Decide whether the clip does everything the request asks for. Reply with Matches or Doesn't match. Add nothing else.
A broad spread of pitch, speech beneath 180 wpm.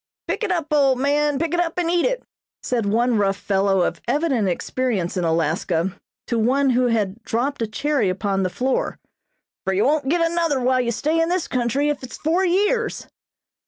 Doesn't match